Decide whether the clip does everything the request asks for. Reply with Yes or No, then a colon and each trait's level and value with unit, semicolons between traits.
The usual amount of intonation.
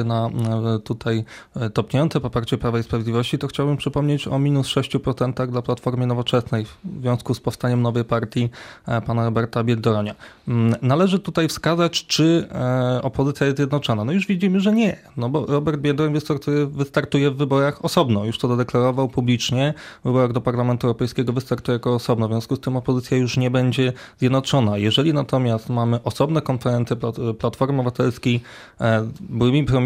Yes: average, 3.1 semitones